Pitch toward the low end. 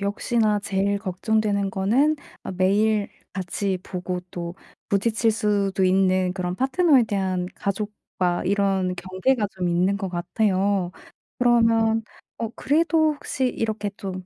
No: high, 200 Hz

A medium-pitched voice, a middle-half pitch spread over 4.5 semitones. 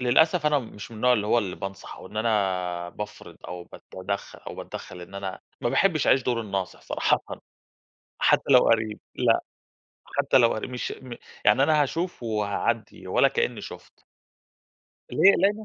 No: low, 115 Hz; wide, 5.6 semitones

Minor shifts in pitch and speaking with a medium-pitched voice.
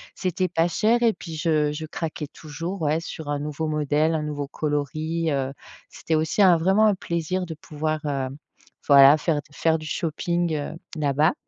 Yes: narrow, 2.3 semitones; medium, 155 Hz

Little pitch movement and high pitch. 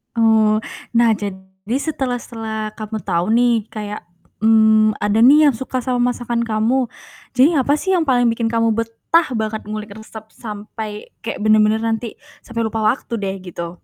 Yes: narrow, 1.9 semitones; high, 220 Hz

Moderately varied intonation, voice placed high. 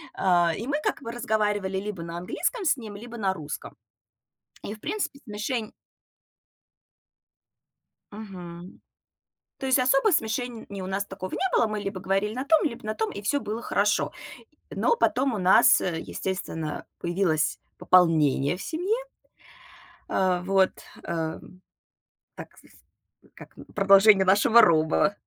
Yes: average, 4.2 semitones; high, 200 Hz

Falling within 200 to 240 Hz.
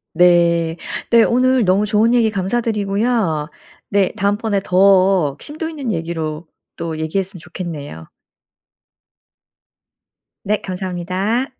No: high, 190 Hz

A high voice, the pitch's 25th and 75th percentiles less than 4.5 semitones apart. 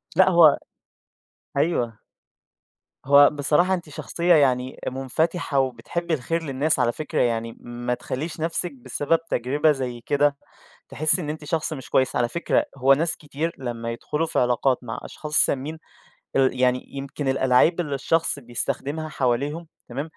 No: medium, 140 Hz; average, 3.9 semitones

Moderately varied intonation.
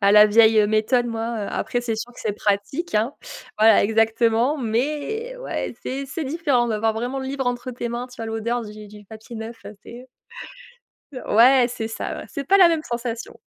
Yes: average, 3.1 semitones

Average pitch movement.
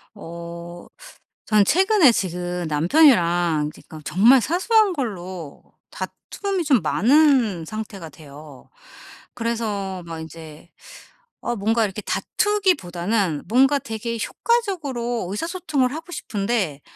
No: wide, 8.4 semitones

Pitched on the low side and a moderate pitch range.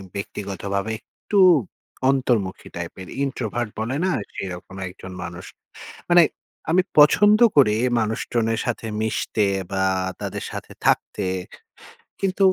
No: low, 110 Hz; wide, 5.8 semitones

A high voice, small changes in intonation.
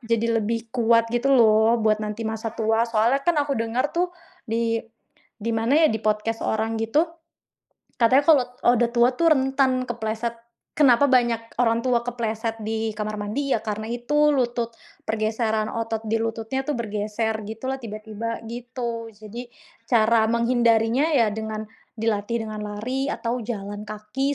Yes: high, 230 Hz; narrow, 1.9 semitones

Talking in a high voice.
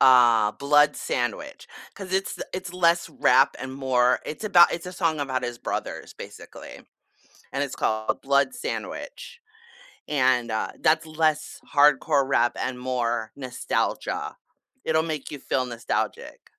No: medium, 140 Hz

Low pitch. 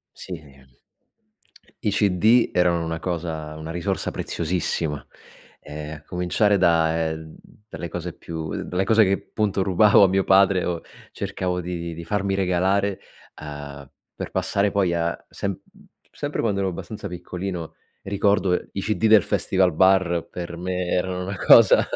Yes: very low, 90 Hz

